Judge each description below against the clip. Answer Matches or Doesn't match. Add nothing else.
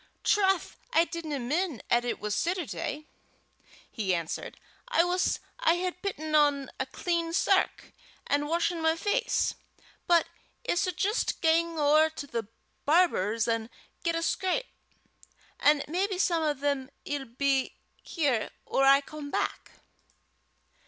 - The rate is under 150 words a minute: Matches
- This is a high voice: Matches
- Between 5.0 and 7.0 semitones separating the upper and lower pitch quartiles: Doesn't match